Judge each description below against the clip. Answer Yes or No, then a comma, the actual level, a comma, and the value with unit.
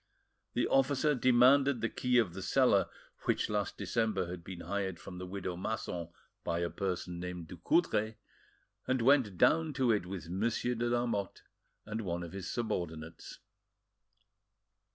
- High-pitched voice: No, low, 100 Hz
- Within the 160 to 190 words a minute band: No, average, 150 wpm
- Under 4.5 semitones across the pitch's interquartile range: No, average, 5.3 semitones